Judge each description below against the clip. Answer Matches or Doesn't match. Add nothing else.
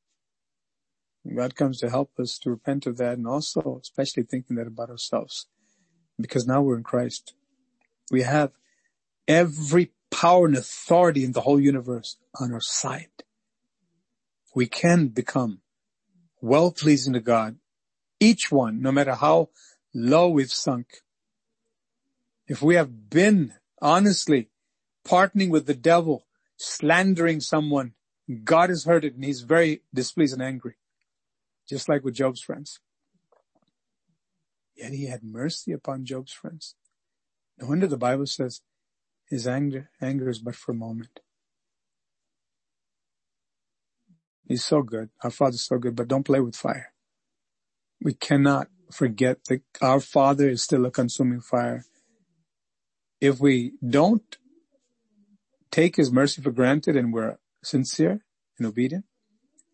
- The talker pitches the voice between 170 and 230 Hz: Doesn't match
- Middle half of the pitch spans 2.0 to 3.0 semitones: Doesn't match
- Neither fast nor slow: Doesn't match